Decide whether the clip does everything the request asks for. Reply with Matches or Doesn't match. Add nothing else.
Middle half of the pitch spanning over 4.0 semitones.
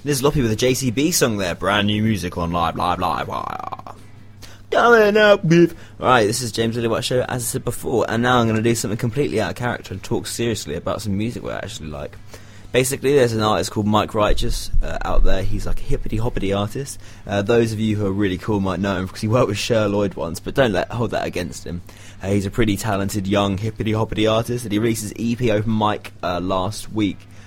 Doesn't match